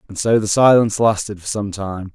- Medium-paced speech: No, fast, 225 wpm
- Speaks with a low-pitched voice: Yes, low, 105 Hz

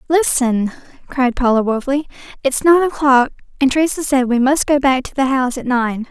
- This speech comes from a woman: Yes, female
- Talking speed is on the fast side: No, average, 185 wpm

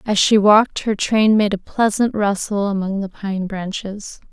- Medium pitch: No, high, 205 Hz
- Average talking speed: Yes, average, 180 wpm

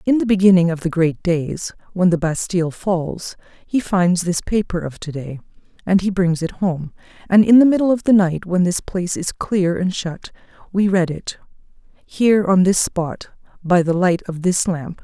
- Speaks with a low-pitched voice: No, medium, 180 Hz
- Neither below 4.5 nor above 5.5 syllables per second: Yes, 4.7 syllables/s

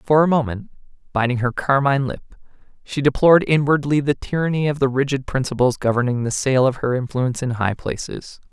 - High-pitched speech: No, low, 135 Hz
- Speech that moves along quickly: No, average, 175 wpm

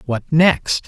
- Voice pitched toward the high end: No, low, 135 Hz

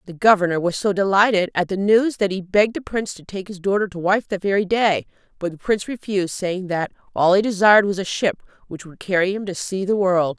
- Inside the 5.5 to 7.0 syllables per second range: Yes, 6.0 syllables/s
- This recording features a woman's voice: Yes, female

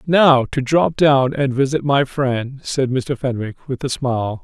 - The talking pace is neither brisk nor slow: Yes, average, 190 wpm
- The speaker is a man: Yes, male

